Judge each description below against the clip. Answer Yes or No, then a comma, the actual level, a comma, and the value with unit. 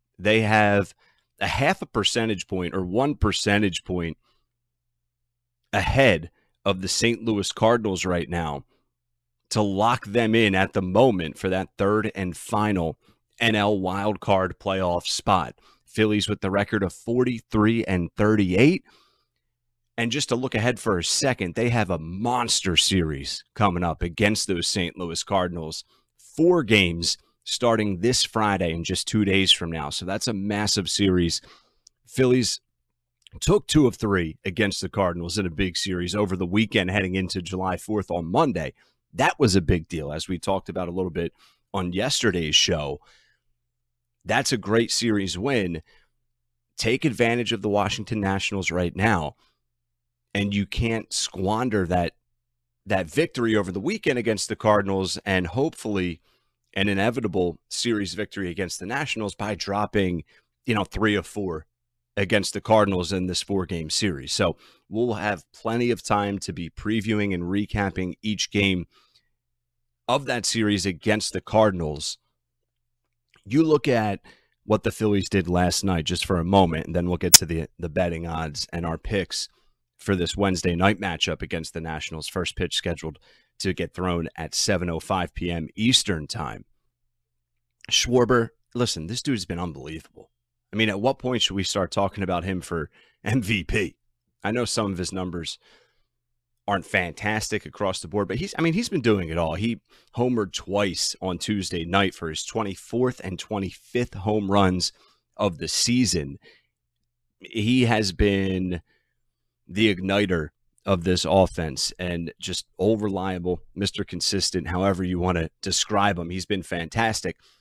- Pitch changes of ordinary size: Yes, average, 4.1 semitones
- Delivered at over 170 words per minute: No, average, 155 wpm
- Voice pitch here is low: Yes, low, 100 Hz